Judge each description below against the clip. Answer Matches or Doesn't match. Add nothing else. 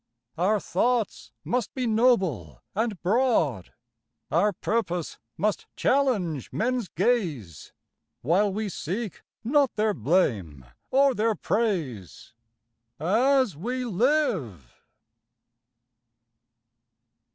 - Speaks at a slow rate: Matches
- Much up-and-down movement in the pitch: Matches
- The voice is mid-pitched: Doesn't match